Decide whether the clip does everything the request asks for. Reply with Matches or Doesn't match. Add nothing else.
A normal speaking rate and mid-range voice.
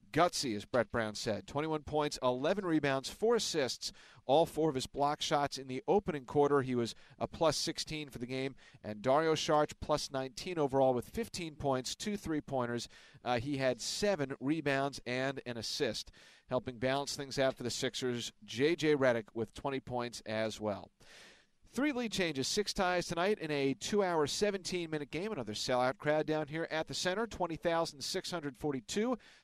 Matches